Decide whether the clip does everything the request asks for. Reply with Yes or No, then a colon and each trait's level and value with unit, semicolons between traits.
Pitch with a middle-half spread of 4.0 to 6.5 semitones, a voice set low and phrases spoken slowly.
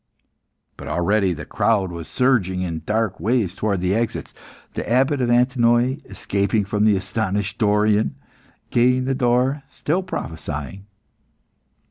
Yes: average, 4.3 semitones; low, 110 Hz; slow, 130 wpm